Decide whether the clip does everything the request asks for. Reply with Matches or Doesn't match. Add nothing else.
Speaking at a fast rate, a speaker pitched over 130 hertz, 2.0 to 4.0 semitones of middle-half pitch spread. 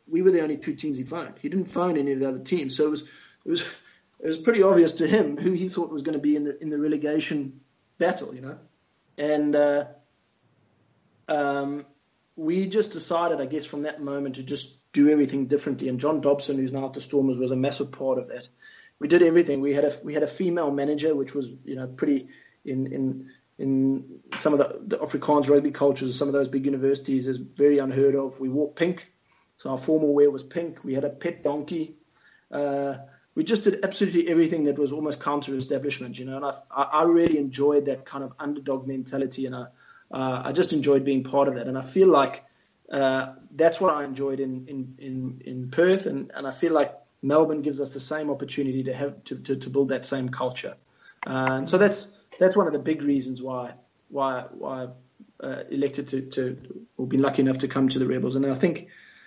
Matches